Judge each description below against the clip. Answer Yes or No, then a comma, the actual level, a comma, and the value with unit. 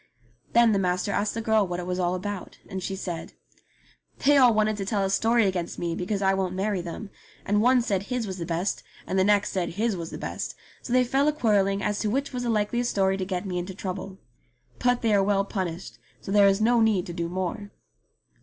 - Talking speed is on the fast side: Yes, fast, 240 wpm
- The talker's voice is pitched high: Yes, high, 200 Hz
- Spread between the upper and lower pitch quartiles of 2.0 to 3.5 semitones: Yes, average, 3.1 semitones